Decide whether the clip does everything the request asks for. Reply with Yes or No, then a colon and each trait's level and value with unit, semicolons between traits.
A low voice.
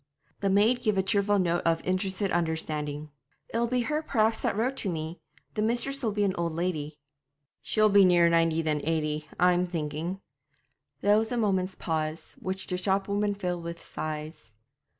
No: medium, 185 Hz